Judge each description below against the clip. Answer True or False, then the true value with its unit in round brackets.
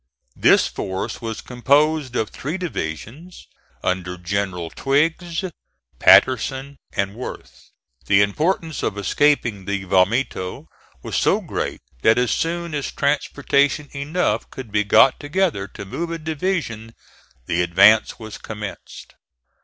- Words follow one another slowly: True (120 wpm)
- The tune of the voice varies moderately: False (7.1 semitones)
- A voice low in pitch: True (125 Hz)